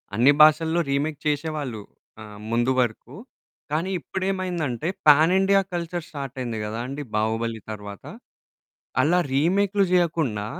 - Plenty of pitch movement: Yes, wide, 6.5 semitones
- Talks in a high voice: No, medium, 150 Hz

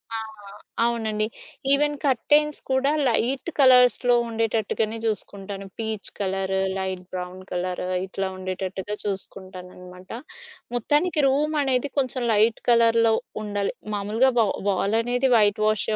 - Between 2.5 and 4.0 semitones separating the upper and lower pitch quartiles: No, average, 4.5 semitones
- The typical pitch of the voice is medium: No, high, 220 Hz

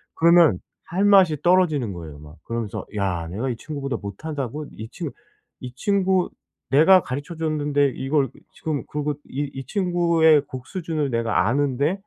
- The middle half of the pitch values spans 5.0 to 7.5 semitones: Yes, wide, 5.5 semitones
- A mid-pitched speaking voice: Yes, medium, 145 Hz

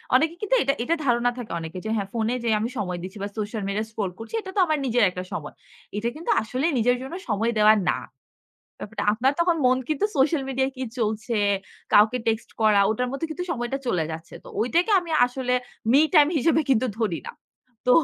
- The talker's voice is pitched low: No, high, 240 Hz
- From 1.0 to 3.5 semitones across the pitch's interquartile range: No, average, 4.1 semitones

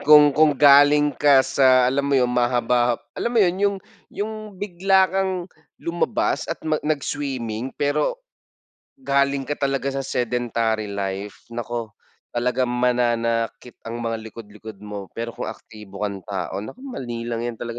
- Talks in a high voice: No, low, 125 Hz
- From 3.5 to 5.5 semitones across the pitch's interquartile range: Yes, average, 3.9 semitones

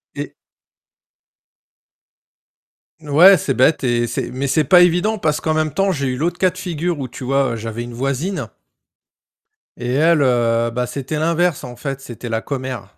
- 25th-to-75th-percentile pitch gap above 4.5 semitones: Yes, average, 5.1 semitones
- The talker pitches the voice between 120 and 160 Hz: Yes, medium, 140 Hz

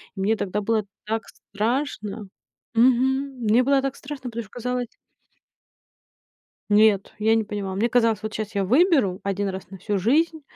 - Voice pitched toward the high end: Yes, high, 225 Hz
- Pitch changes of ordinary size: Yes, average, 3.7 semitones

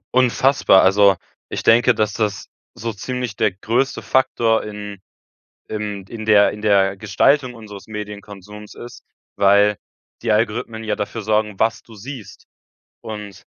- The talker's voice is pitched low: Yes, low, 105 Hz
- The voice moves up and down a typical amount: No, narrow, 2.1 semitones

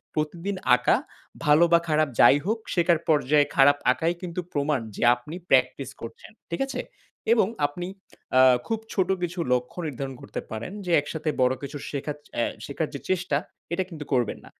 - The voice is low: No, medium, 150 Hz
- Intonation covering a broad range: No, average, 4.0 semitones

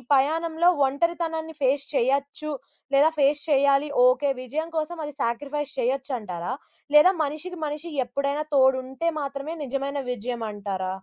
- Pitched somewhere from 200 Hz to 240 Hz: No, very high, 280 Hz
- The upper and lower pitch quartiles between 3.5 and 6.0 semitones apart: No, average, 2.9 semitones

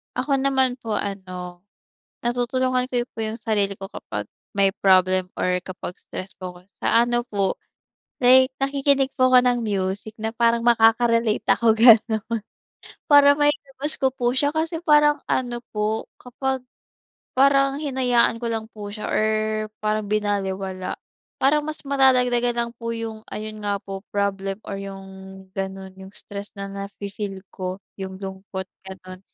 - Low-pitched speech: No, high, 220 Hz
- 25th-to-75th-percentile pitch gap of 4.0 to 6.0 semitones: Yes, average, 4.6 semitones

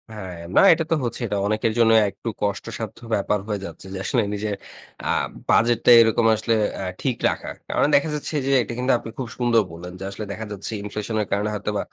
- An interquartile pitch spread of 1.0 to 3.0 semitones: Yes, narrow, 2.5 semitones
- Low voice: Yes, low, 110 Hz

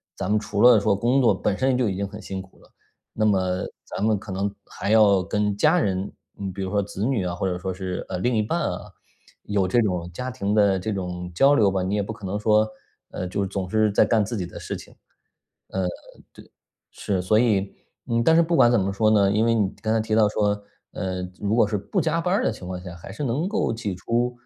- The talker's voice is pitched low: Yes, low, 105 Hz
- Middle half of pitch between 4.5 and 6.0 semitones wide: No, average, 3.1 semitones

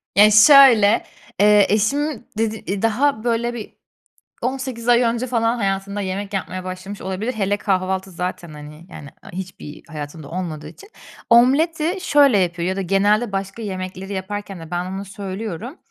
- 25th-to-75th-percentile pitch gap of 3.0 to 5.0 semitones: Yes, average, 3.8 semitones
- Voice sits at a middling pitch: No, high, 200 Hz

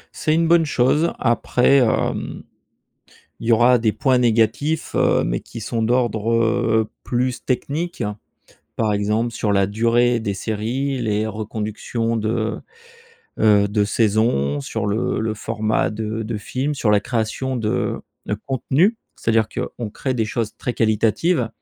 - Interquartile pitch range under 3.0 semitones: Yes, narrow, 2.5 semitones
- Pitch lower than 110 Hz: No, low, 115 Hz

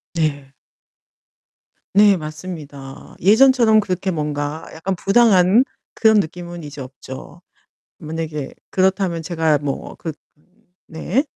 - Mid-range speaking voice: Yes, medium, 170 Hz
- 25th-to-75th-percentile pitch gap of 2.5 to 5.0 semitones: Yes, average, 4.3 semitones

